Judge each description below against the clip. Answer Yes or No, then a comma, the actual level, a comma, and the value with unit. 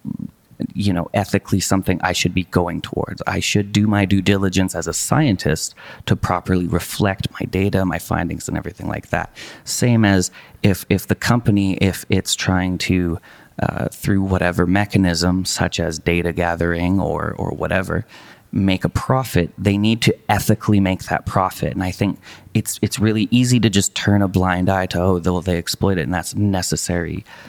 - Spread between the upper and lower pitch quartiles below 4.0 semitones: Yes, narrow, 2.5 semitones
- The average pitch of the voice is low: Yes, very low, 95 Hz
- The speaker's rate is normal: Yes, average, 180 wpm